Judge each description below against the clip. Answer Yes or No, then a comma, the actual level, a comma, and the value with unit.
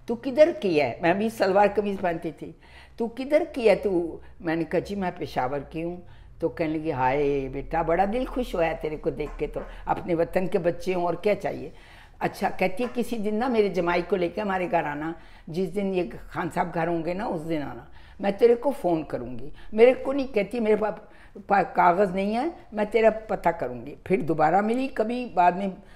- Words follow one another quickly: Yes, fast, 215 wpm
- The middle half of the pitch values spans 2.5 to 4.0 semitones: No, average, 5.0 semitones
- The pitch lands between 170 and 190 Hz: Yes, medium, 185 Hz